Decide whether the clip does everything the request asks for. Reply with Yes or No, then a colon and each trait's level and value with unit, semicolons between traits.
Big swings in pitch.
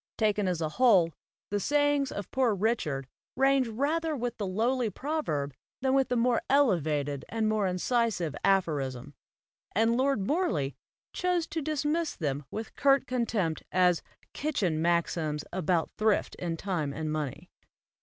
Yes: wide, 8.2 semitones